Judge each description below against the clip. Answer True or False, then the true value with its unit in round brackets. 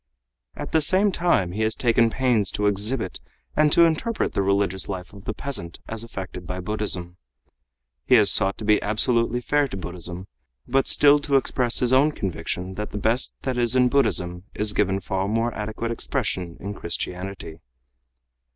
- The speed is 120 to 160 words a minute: False (175 wpm)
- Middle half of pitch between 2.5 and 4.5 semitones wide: False (4.9 semitones)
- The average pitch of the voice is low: True (105 Hz)